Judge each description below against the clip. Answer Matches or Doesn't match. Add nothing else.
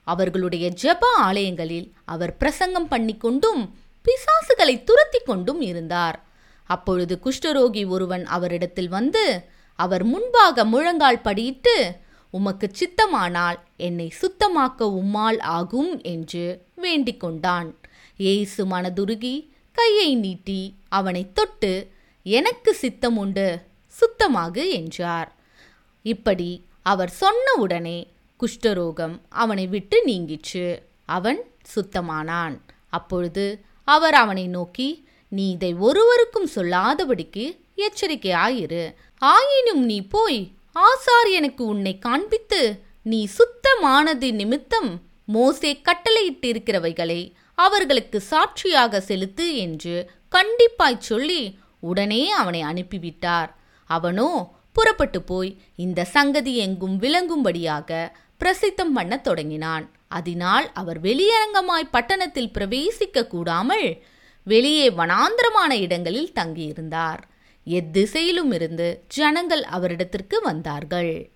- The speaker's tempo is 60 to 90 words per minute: Matches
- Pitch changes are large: Matches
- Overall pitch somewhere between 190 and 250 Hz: Matches